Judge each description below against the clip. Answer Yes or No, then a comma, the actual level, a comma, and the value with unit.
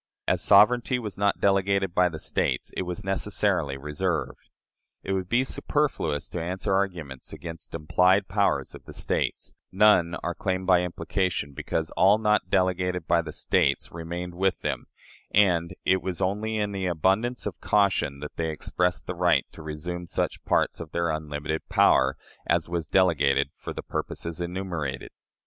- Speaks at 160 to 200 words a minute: Yes, average, 165 wpm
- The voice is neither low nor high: No, very low, 90 Hz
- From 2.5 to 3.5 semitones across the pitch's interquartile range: Yes, average, 2.9 semitones